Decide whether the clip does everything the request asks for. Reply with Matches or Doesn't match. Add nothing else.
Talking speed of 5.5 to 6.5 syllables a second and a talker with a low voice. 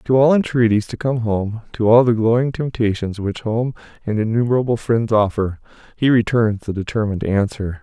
Doesn't match